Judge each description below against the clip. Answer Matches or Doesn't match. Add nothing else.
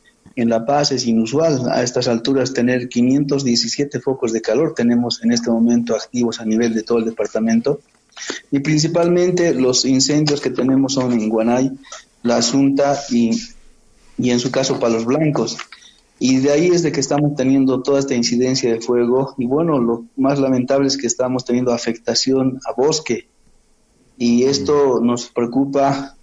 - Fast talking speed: Doesn't match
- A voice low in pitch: Matches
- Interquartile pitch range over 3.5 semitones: Doesn't match